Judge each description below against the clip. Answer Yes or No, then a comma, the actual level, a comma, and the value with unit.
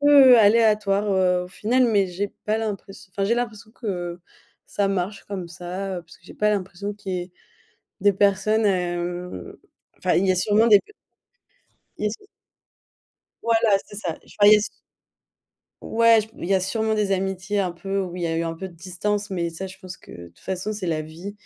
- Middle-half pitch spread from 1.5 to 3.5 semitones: Yes, average, 2.9 semitones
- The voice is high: Yes, high, 195 Hz